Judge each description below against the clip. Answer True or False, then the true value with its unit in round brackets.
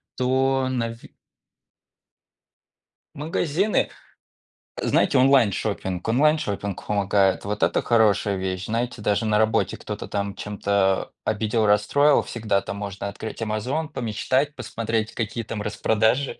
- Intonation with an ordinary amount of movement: True (4.0 semitones)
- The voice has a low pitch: True (110 Hz)